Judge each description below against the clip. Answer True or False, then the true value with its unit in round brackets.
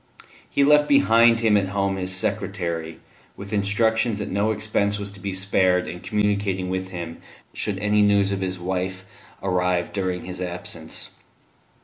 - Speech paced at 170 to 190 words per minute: False (155 wpm)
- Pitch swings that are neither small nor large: False (2.2 semitones)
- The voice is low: True (100 Hz)